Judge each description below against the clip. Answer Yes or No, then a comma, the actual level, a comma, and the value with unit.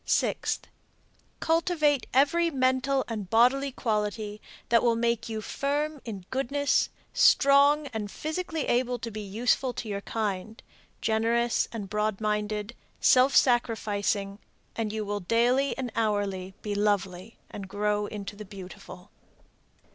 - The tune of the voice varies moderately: Yes, average, 4.0 semitones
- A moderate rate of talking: No, slow, 130 wpm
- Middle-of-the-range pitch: No, high, 225 Hz